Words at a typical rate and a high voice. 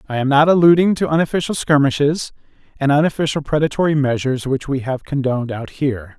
No: average, 165 wpm; medium, 140 Hz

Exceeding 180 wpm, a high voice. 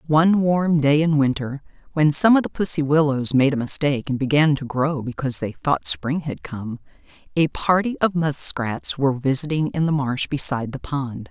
No: average, 190 wpm; medium, 145 Hz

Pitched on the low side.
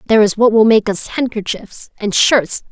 No: high, 215 Hz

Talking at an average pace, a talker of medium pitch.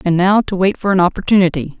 No: fast, 235 wpm; medium, 180 Hz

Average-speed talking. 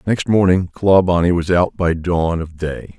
Yes: average, 180 wpm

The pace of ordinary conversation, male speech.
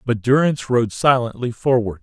Yes: average, 150 wpm; male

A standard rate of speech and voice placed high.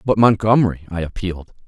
No: average, 145 wpm; low, 100 Hz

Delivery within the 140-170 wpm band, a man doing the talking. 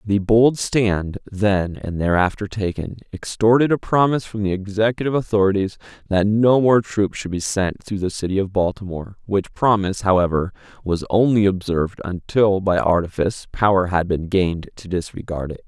Yes: average, 160 wpm; male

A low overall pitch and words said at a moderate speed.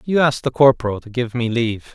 No: low, 125 Hz; fast, 245 wpm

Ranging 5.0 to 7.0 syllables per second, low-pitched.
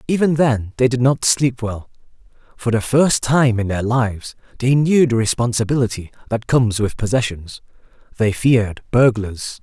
No: 4.8 syllables/s; low, 120 Hz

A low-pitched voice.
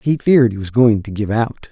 Yes: low, 115 Hz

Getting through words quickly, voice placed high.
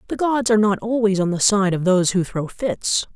Yes: fast, 245 wpm; high, 200 Hz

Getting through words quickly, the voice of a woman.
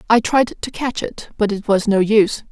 Yes: fast, 240 wpm; female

